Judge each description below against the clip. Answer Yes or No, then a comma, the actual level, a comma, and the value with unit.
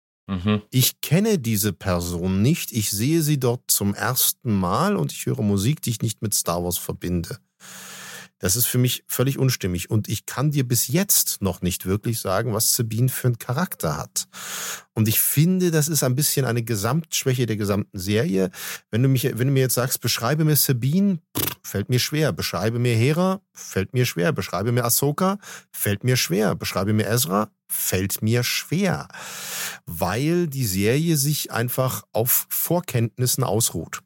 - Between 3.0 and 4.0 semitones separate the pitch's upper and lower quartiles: No, average, 5.2 semitones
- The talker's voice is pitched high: No, low, 120 Hz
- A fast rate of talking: No, average, 170 wpm